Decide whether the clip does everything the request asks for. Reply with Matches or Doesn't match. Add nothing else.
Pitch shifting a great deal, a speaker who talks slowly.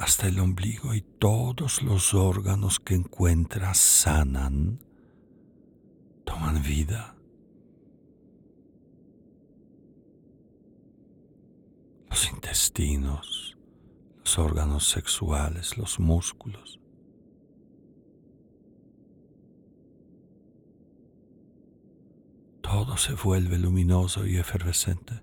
Doesn't match